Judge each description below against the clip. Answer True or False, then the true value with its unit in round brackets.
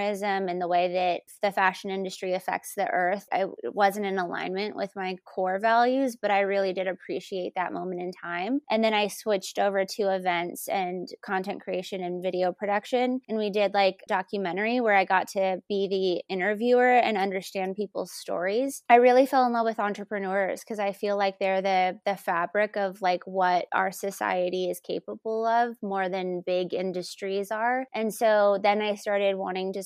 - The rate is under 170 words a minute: False (185 wpm)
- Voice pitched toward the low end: False (195 Hz)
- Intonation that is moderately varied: False (2.1 semitones)